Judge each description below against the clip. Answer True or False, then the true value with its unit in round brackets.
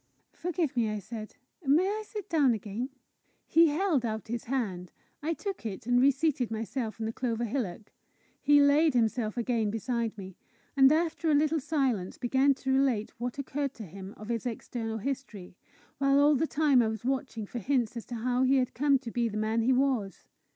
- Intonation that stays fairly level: False (4.1 semitones)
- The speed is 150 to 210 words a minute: True (195 wpm)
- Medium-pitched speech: False (250 Hz)